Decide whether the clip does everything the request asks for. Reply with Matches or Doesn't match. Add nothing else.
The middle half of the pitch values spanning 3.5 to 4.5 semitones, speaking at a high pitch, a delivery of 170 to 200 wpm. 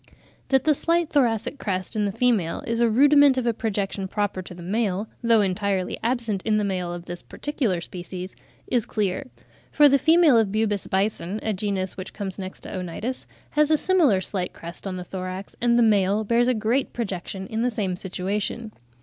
Matches